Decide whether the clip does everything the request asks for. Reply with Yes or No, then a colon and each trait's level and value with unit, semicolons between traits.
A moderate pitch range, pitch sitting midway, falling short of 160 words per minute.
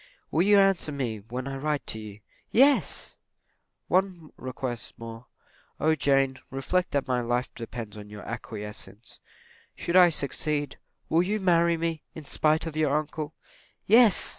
No: wide, 5.8 semitones; medium, 145 Hz; average, 150 wpm